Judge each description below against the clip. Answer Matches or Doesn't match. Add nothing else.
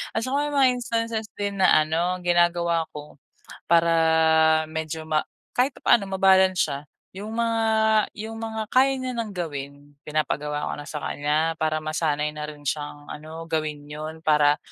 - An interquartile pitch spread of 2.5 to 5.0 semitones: Doesn't match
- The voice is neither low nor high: Matches